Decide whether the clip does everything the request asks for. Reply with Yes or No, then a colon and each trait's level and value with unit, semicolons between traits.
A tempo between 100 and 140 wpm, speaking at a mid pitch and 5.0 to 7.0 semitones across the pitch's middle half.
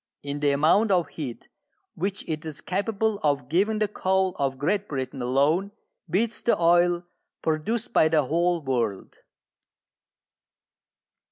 Yes: slow, 135 wpm; medium, 165 Hz; wide, 5.5 semitones